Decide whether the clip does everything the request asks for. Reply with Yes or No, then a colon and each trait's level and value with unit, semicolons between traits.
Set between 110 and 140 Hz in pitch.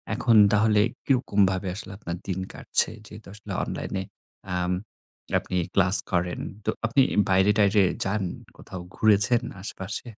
No: low, 100 Hz